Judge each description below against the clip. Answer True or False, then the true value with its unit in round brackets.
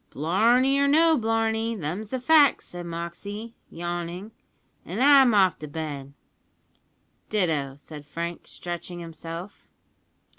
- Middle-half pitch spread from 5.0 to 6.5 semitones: True (5.5 semitones)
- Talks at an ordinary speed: False (115 wpm)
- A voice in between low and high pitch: True (180 Hz)